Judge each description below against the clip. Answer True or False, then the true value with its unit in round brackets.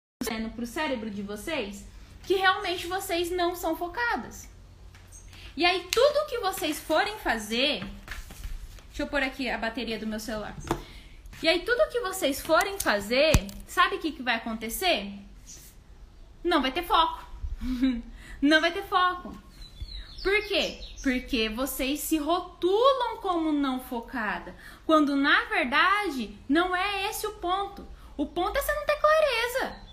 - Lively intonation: True (7.1 semitones)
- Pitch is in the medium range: False (305 Hz)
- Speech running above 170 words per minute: False (140 wpm)